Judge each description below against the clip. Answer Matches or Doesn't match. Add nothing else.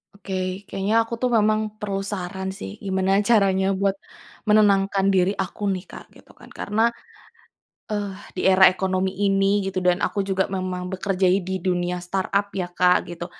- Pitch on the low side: Doesn't match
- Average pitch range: Doesn't match